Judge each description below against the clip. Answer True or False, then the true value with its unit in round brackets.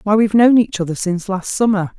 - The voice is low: False (200 Hz)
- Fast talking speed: True (240 wpm)